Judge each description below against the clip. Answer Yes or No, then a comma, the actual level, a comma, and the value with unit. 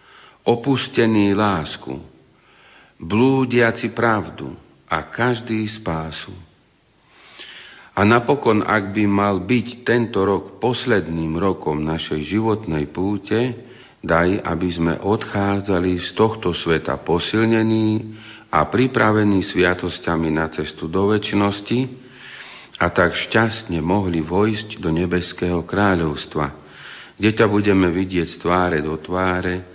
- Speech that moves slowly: Yes, slow, 105 wpm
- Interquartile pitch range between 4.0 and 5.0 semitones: Yes, average, 4.7 semitones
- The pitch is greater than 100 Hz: No, very low, 95 Hz